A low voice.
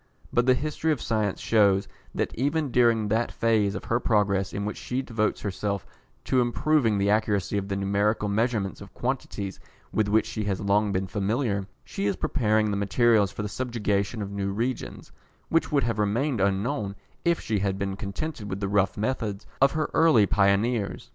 Yes: low, 105 Hz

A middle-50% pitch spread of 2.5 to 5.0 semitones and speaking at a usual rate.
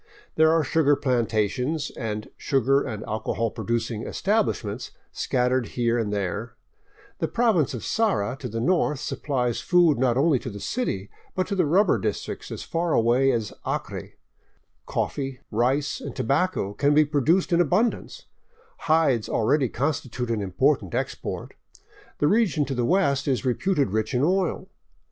No: wide, 5.5 semitones; average, 155 wpm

